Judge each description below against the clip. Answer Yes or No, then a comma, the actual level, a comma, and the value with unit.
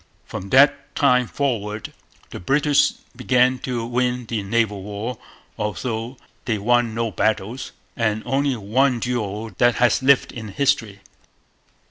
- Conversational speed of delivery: No, slow, 130 wpm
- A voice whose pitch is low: Yes, low, 120 Hz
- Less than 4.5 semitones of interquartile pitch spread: Yes, average, 2.9 semitones